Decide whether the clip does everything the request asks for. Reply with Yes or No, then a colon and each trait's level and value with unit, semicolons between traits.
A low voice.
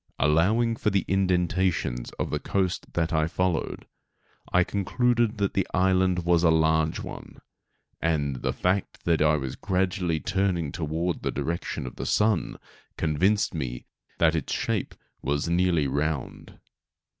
Yes: very low, 85 Hz